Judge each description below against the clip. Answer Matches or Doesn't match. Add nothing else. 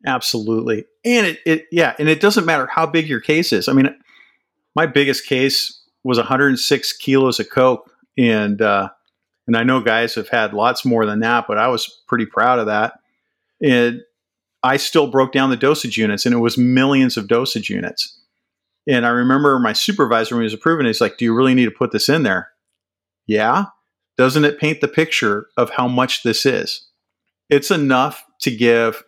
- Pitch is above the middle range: Doesn't match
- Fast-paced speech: Doesn't match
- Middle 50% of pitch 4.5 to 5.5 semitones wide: Doesn't match